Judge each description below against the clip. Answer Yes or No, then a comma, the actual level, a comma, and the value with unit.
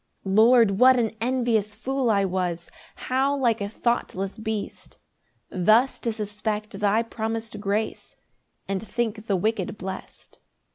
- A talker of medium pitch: No, high, 220 Hz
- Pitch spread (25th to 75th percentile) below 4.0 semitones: Yes, average, 2.8 semitones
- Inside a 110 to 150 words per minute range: Yes, slow, 135 wpm